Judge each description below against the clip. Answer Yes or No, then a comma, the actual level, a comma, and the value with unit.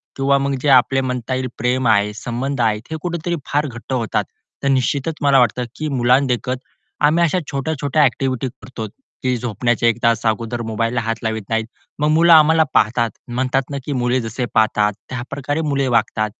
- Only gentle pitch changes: No, average, 3.1 semitones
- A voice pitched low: Yes, low, 125 Hz